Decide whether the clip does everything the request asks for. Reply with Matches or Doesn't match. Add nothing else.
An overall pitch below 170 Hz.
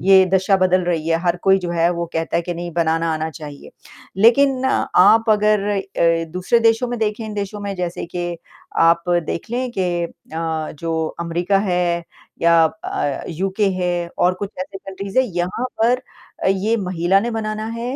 Doesn't match